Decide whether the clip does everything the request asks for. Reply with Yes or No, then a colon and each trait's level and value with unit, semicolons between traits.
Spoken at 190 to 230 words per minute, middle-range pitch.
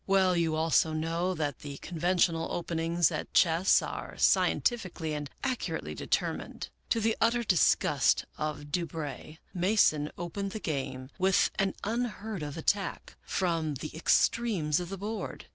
No: average, 150 wpm; medium, 170 Hz